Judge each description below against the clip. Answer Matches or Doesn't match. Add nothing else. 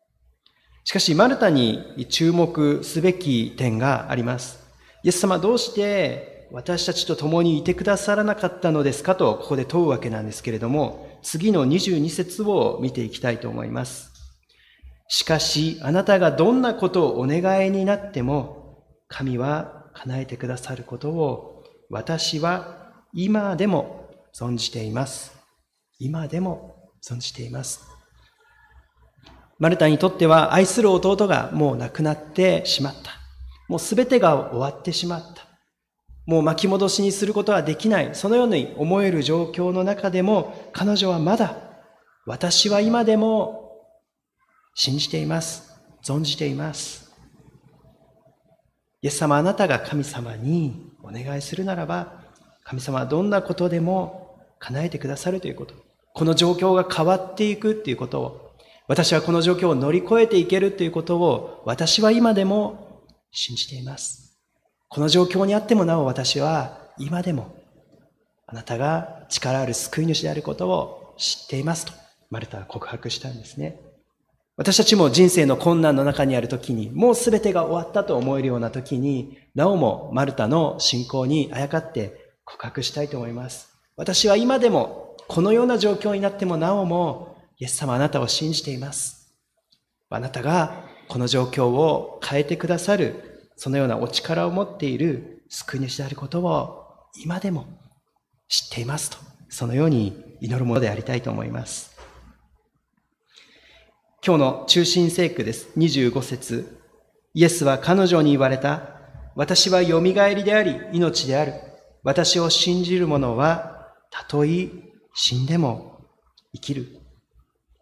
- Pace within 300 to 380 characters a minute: Doesn't match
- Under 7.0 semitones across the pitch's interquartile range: Matches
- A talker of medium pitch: Matches